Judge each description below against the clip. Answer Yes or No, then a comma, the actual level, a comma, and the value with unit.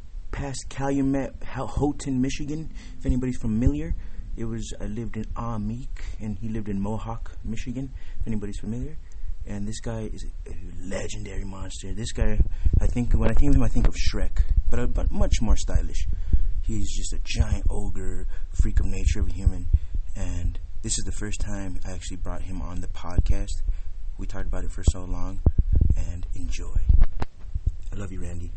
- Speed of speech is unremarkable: Yes, average, 180 wpm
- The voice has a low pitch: Yes, very low, 95 Hz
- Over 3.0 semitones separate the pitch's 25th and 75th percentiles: Yes, average, 4.4 semitones